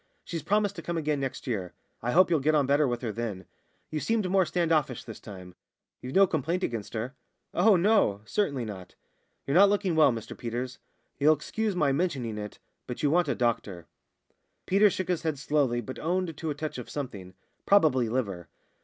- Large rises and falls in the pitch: Yes, wide, 6.7 semitones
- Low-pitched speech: No, medium, 145 Hz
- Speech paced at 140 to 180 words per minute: No, average, 200 wpm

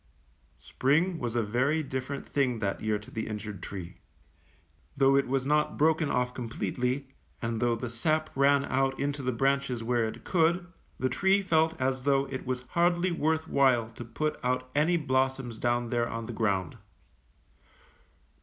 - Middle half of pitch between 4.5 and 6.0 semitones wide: No, average, 3.7 semitones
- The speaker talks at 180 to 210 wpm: No, average, 170 wpm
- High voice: No, low, 130 Hz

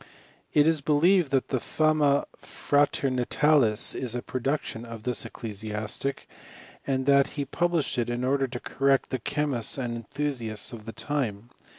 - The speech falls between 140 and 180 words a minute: Yes, average, 155 wpm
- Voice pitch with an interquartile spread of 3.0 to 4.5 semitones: Yes, average, 3.7 semitones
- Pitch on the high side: No, low, 130 Hz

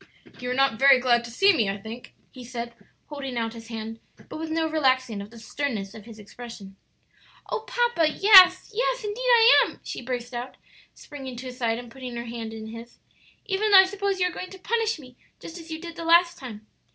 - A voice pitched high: Yes, very high, 260 Hz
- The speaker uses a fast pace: Yes, fast, 225 wpm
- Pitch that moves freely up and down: Yes, wide, 7.3 semitones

